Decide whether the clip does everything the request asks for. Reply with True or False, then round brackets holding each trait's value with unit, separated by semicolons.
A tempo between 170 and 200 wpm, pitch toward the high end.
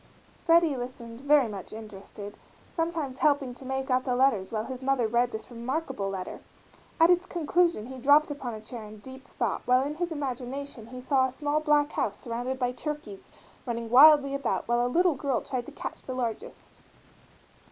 True (185 wpm; 260 Hz)